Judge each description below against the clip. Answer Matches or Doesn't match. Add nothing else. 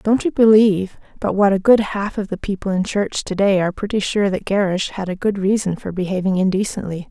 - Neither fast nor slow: Doesn't match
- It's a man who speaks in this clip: Doesn't match